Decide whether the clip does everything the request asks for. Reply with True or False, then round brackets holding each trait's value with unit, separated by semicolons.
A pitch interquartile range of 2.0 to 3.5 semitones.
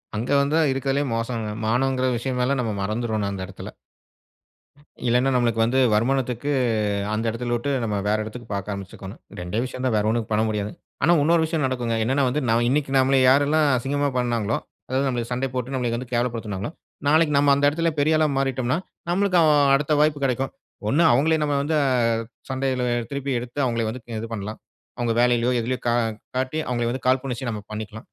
True (3.2 semitones)